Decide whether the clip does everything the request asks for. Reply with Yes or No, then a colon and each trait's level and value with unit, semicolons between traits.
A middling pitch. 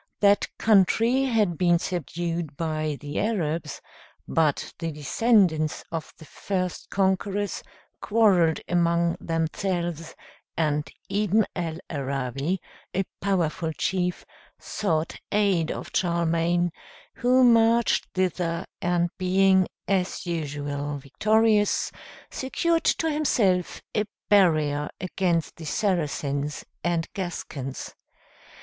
Yes: medium, 175 Hz